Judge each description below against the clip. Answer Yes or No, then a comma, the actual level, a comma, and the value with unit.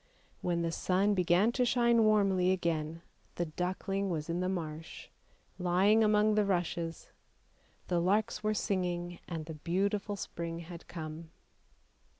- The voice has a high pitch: No, medium, 180 Hz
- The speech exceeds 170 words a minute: No, average, 140 wpm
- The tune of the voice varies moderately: Yes, average, 3.2 semitones